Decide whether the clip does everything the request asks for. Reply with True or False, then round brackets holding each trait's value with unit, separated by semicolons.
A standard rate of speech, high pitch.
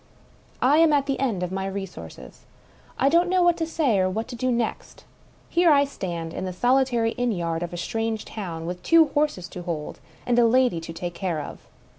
False (220 wpm; 225 Hz)